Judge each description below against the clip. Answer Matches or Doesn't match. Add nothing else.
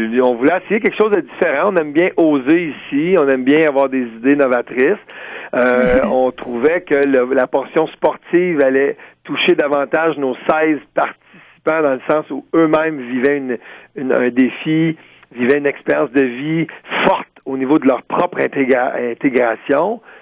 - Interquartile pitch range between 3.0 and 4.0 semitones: Matches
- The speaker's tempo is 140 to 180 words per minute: Matches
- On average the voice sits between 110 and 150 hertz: Matches